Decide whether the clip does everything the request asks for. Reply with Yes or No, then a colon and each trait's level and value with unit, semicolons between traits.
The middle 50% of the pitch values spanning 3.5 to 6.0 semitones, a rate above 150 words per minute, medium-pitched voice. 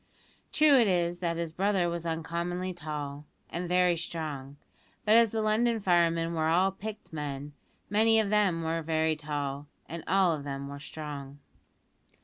Yes: average, 4.1 semitones; average, 160 wpm; medium, 170 Hz